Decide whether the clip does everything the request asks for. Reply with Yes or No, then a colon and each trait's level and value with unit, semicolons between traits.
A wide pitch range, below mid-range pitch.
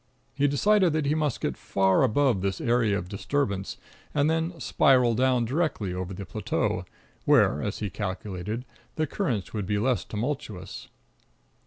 Yes: wide, 6.5 semitones; low, 120 Hz